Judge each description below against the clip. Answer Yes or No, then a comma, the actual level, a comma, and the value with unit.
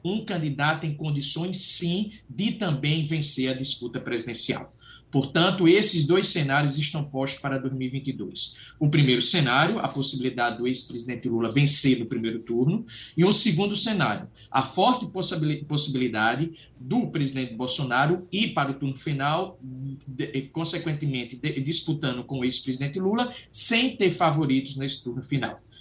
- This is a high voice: No, medium, 145 Hz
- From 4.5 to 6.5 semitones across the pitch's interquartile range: Yes, average, 4.8 semitones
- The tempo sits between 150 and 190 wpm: No, average, 135 wpm